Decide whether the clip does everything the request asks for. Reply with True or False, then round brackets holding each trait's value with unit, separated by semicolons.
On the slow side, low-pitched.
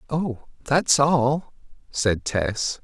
True (85 wpm; 130 Hz)